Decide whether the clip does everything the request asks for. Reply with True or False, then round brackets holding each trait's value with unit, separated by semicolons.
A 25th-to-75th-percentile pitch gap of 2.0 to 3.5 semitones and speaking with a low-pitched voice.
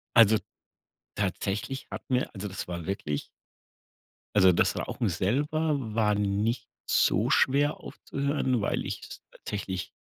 False (5.3 semitones; 105 Hz)